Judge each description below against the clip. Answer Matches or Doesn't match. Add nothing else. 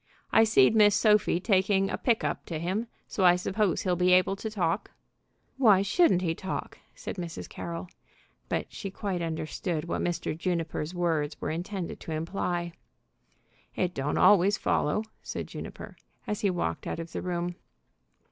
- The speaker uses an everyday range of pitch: Matches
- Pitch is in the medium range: Matches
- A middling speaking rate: Matches